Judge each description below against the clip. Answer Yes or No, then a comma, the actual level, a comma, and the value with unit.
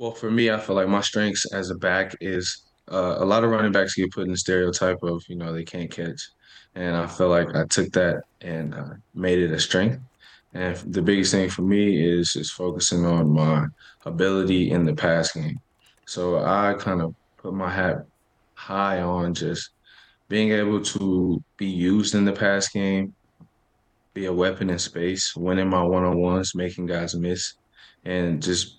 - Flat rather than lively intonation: Yes, narrow, 2.3 semitones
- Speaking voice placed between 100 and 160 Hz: No, very low, 90 Hz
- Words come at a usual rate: Yes, average, 190 wpm